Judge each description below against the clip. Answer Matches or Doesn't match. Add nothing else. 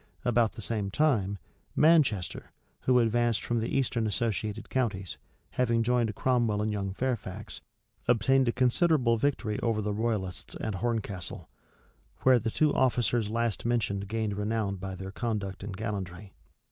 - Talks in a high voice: Doesn't match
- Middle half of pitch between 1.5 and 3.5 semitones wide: Matches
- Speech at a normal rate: Matches